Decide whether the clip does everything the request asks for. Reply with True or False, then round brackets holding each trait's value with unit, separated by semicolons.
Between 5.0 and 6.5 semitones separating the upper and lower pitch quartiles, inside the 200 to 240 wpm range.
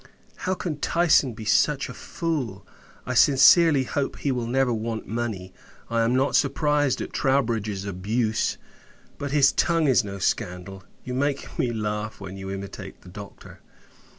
False (5.5 semitones; 155 wpm)